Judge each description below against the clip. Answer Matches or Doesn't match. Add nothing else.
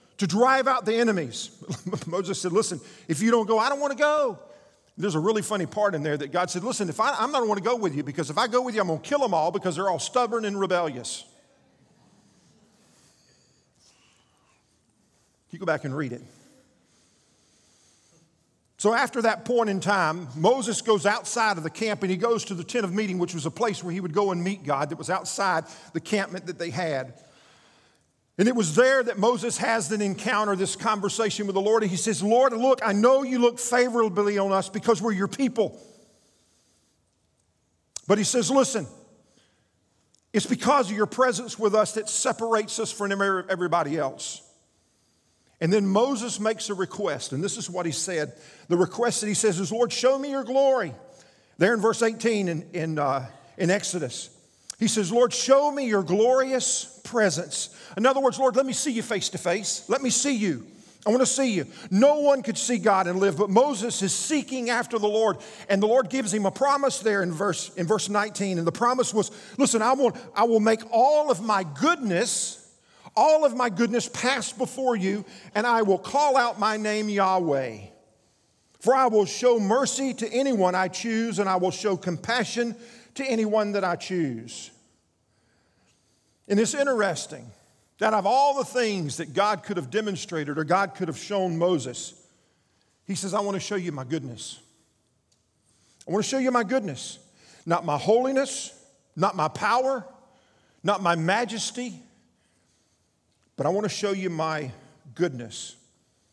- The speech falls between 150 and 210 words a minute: Matches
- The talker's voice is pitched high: Matches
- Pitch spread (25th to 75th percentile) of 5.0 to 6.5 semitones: Matches